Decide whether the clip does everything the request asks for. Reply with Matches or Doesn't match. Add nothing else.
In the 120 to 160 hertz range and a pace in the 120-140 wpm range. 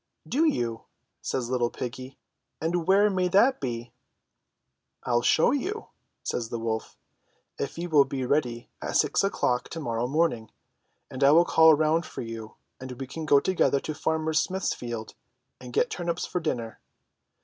Doesn't match